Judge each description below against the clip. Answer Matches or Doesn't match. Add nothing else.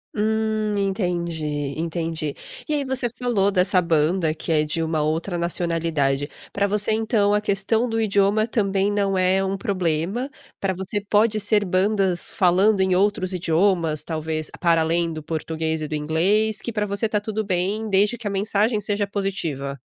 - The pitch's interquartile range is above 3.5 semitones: Matches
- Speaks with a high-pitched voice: Matches